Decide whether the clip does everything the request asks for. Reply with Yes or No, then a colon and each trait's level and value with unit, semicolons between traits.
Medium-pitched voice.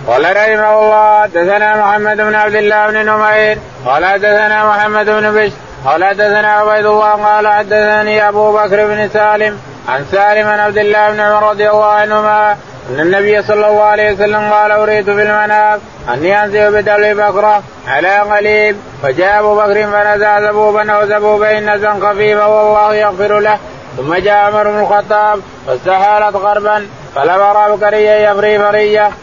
No: high, 210 Hz